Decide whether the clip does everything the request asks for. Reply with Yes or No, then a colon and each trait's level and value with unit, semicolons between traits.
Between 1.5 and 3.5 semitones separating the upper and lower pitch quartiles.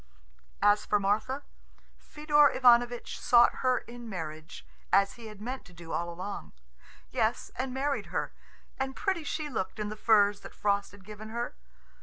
No: average, 4.2 semitones